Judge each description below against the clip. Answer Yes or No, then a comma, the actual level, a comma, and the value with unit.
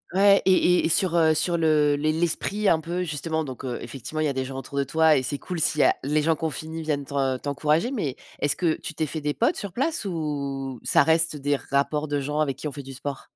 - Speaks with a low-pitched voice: No, medium, 155 Hz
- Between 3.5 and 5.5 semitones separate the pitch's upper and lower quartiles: No, average, 2.7 semitones